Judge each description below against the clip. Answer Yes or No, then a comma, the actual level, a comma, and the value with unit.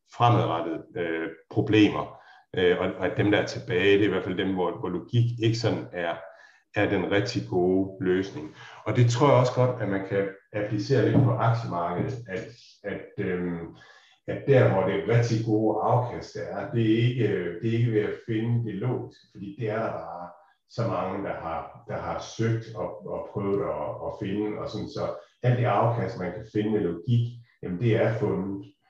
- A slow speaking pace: No, average, 205 wpm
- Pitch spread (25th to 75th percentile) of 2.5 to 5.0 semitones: Yes, average, 3.1 semitones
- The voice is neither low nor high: No, low, 110 Hz